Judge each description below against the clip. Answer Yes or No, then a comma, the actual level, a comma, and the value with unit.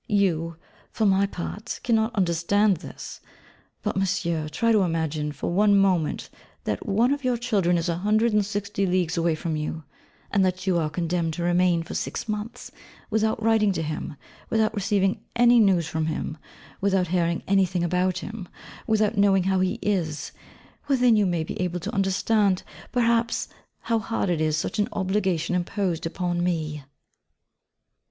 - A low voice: No, high, 190 Hz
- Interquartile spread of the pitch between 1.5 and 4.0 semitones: Yes, average, 3.7 semitones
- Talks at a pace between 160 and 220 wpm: Yes, average, 165 wpm